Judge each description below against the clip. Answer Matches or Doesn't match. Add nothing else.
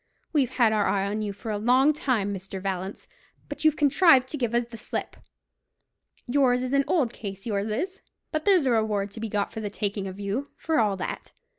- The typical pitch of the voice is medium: Doesn't match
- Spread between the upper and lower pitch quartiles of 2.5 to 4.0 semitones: Doesn't match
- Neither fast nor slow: Doesn't match